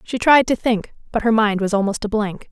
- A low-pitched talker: No, high, 220 Hz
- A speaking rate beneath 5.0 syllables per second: No, 5.4 syllables/s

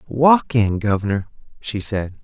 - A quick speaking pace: No, slow, 135 wpm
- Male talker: Yes, male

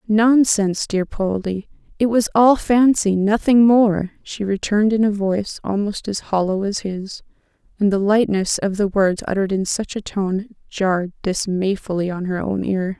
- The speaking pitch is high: Yes, high, 200 Hz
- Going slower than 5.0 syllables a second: Yes, 4.6 syllables/s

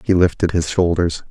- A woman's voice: No, male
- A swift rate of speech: No, average, 185 wpm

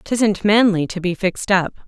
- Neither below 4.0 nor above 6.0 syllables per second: Yes, 4.7 syllables/s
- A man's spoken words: No, female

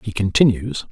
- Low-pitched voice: Yes, low, 105 Hz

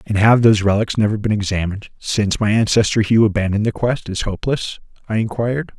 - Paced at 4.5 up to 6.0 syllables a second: No, 6.4 syllables/s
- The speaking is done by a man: Yes, male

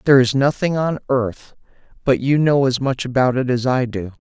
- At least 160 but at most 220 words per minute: Yes, average, 200 wpm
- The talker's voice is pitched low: Yes, low, 130 Hz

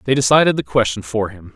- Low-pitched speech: Yes, low, 115 Hz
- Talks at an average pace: No, fast, 230 wpm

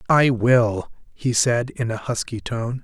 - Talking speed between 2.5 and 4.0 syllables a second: Yes, 3.7 syllables/s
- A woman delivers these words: No, male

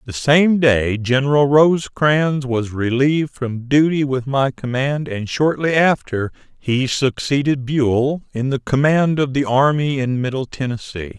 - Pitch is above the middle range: No, low, 135 Hz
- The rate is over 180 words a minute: No, average, 145 wpm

